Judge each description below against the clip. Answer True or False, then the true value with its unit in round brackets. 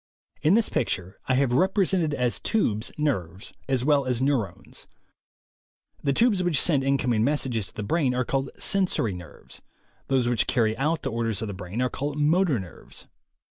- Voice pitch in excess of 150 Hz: False (130 Hz)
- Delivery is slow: False (175 wpm)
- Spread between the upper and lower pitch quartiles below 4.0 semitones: False (5.2 semitones)